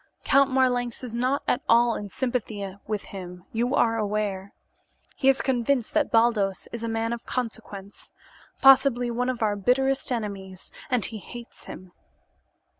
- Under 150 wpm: No, average, 155 wpm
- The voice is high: Yes, high, 230 Hz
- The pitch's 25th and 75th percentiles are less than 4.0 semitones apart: Yes, average, 3.4 semitones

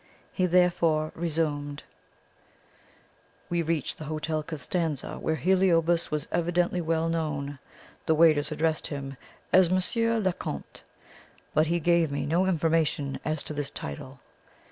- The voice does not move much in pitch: Yes, narrow, 2.3 semitones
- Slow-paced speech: Yes, slow, 130 wpm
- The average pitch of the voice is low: No, medium, 160 Hz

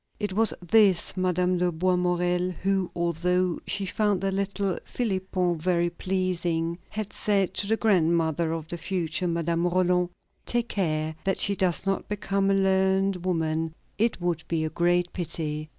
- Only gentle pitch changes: Yes, narrow, 2.3 semitones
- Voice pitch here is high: No, medium, 180 Hz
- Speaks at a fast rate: No, average, 155 wpm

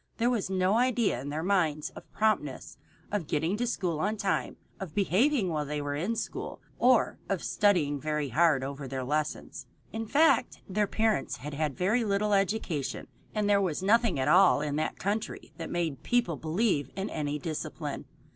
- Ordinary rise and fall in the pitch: No, wide, 6.0 semitones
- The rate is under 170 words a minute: No, average, 175 wpm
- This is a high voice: No, medium, 180 Hz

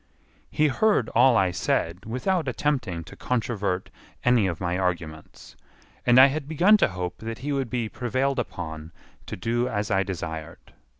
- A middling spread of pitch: No, wide, 6.5 semitones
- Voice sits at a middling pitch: No, low, 115 Hz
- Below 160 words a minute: No, average, 165 wpm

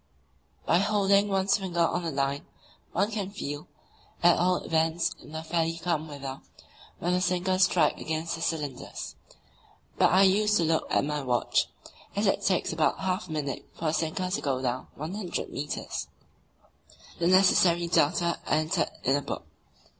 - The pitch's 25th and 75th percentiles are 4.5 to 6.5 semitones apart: No, average, 3.3 semitones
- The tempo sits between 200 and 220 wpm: No, average, 165 wpm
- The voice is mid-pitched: Yes, medium, 170 Hz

